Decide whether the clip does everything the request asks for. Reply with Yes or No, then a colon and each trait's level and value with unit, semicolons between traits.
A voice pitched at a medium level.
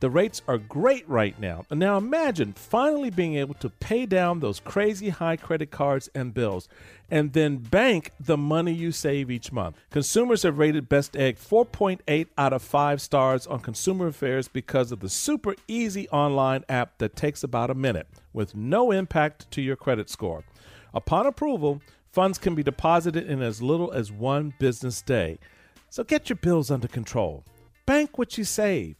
Yes: medium, 145 Hz